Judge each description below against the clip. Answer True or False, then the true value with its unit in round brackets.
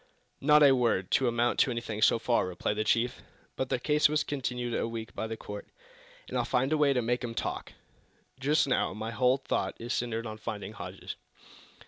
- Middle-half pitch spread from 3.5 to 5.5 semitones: False (2.9 semitones)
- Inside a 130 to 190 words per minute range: False (205 wpm)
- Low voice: True (120 Hz)